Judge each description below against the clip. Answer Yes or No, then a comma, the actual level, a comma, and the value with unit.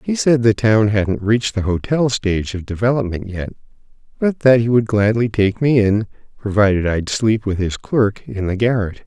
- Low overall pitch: Yes, low, 110 Hz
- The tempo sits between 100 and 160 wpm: No, average, 190 wpm